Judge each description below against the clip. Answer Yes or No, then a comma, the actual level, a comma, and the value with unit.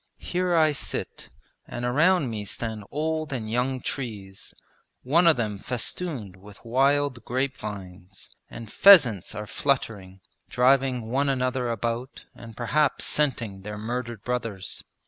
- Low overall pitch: Yes, low, 120 Hz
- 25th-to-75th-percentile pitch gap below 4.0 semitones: No, average, 4.5 semitones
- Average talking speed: No, slow, 130 wpm